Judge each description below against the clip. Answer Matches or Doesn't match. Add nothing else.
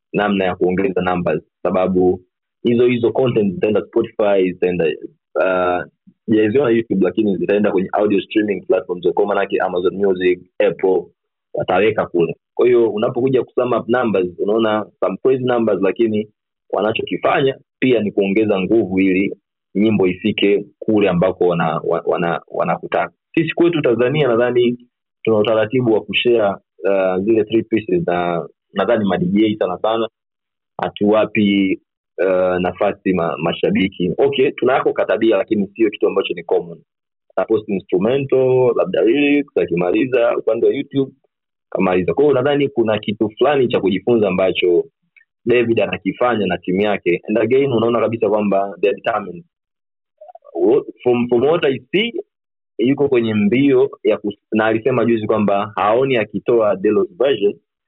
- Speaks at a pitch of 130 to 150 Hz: Doesn't match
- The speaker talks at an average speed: Matches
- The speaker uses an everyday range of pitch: Doesn't match